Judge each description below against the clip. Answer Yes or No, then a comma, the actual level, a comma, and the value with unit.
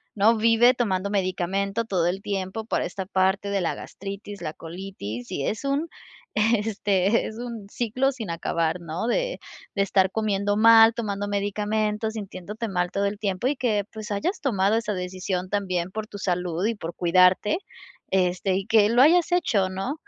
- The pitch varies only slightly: No, average, 3.1 semitones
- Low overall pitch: No, high, 200 Hz